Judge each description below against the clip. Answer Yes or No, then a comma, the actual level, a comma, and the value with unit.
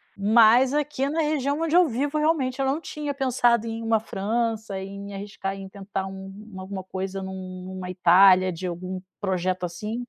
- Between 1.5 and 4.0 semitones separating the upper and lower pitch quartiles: No, average, 5.2 semitones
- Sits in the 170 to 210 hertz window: Yes, high, 200 Hz